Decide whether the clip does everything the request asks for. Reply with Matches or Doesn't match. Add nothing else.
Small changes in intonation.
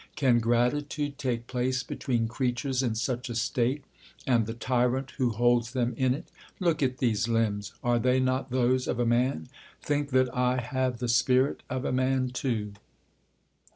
Matches